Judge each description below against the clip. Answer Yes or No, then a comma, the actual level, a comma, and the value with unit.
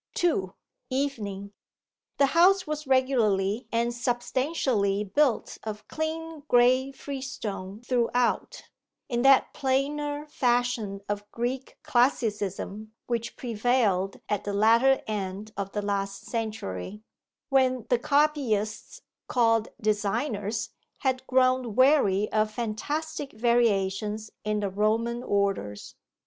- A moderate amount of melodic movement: Yes, average, 4.1 semitones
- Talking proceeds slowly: Yes, slow, 105 wpm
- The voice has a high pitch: Yes, high, 235 Hz